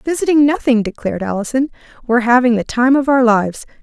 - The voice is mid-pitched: No, high, 245 Hz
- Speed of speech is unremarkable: Yes, average, 175 wpm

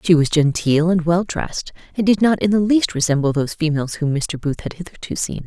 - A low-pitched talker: No, medium, 165 Hz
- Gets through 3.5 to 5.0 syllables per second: No, 5.6 syllables/s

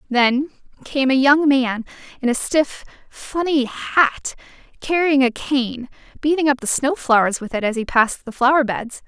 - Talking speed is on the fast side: No, average, 170 wpm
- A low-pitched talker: No, very high, 265 Hz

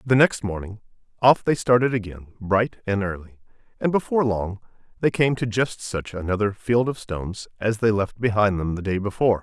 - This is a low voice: Yes, low, 110 Hz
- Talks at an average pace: Yes, average, 190 wpm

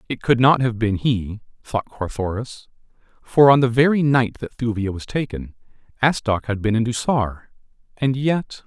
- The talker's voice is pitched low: Yes, low, 120 Hz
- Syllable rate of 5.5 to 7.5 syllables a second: No, 4.7 syllables/s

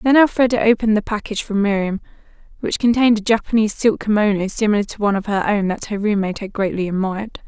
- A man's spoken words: No, female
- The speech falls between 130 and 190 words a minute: No, average, 200 wpm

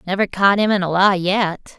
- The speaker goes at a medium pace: No, fast, 235 wpm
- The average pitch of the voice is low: No, high, 190 Hz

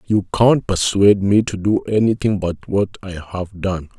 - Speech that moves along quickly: No, average, 180 wpm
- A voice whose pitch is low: Yes, low, 100 Hz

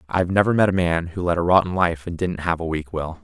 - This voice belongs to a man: Yes, male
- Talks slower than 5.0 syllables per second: No, 6.3 syllables/s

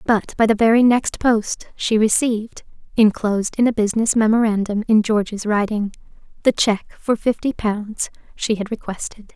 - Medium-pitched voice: No, high, 215 Hz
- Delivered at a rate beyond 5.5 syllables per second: No, 4.9 syllables/s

